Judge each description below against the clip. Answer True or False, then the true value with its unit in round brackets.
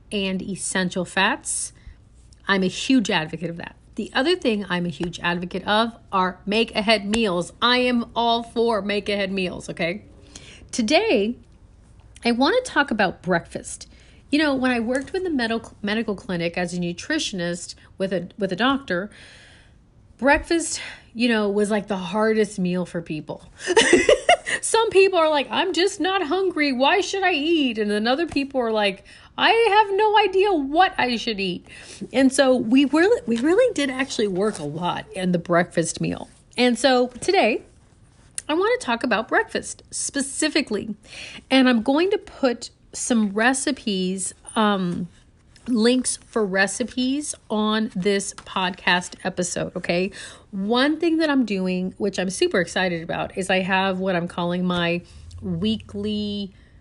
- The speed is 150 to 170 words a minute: True (155 wpm)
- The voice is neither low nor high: False (220 Hz)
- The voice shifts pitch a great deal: True (6.9 semitones)